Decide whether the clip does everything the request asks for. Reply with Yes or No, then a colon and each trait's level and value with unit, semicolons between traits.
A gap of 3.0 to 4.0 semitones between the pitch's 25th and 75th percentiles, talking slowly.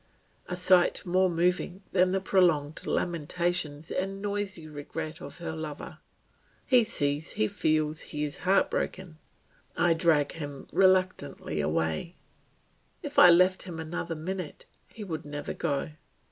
Yes: average, 3.7 semitones; slow, 130 wpm